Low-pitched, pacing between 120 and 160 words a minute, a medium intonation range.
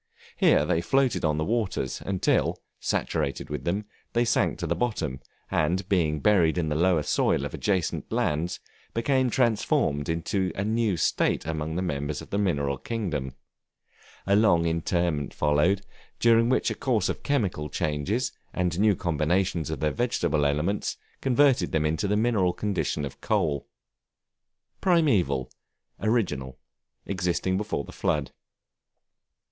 No: very low, 90 Hz; average, 140 wpm; wide, 5.8 semitones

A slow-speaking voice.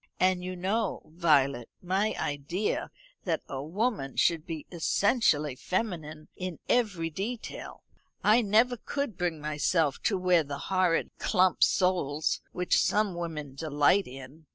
Yes: slow, 130 wpm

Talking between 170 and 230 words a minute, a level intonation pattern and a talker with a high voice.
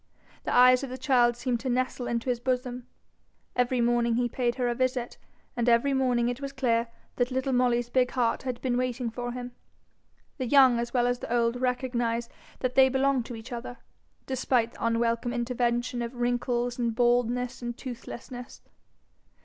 Yes: average, 180 wpm; narrow, 1.1 semitones; high, 245 Hz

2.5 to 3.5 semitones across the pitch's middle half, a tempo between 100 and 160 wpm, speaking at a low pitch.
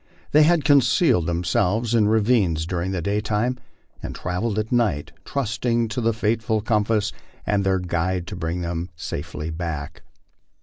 No: average, 4.8 semitones; average, 145 wpm; low, 105 Hz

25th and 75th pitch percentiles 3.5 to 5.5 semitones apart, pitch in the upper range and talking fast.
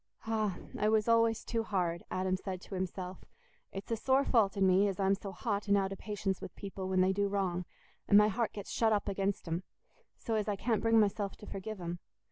No: narrow, 2.4 semitones; high, 200 Hz; fast, 230 wpm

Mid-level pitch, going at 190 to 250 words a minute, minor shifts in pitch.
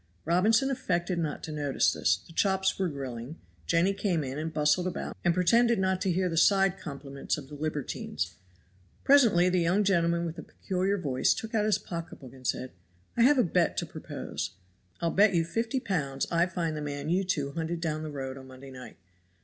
No: medium, 170 Hz; average, 200 wpm; average, 4.7 semitones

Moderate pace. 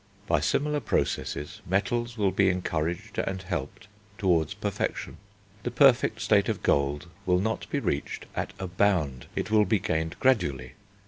Yes: average, 150 wpm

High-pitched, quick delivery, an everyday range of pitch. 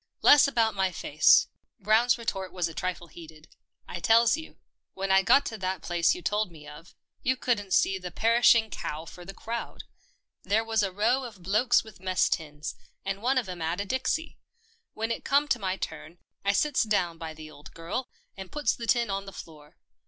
Yes: high, 195 Hz; fast, 215 wpm; average, 5.0 semitones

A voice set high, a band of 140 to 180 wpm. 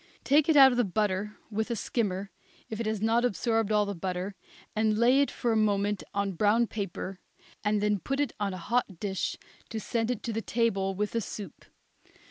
No: high, 215 Hz; fast, 205 wpm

